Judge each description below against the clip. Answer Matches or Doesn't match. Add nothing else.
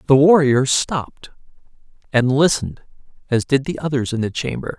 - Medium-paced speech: Matches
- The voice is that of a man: Matches